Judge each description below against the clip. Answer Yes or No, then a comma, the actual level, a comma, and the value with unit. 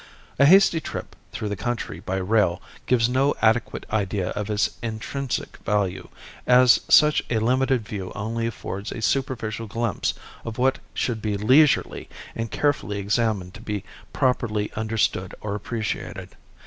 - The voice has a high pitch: No, low, 110 Hz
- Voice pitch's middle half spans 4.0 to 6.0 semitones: No, average, 3.3 semitones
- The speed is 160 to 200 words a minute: No, average, 145 wpm